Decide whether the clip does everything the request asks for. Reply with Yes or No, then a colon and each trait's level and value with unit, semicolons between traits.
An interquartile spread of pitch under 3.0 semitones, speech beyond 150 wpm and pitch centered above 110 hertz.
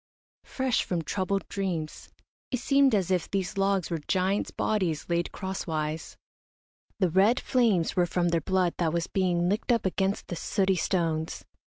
Yes: narrow, 2.6 semitones; average, 160 wpm; medium, 185 Hz